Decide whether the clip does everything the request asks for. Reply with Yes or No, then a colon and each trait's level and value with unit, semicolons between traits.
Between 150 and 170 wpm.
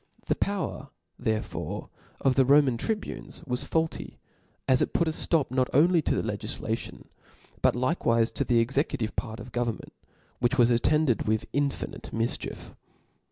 Yes: average, 155 wpm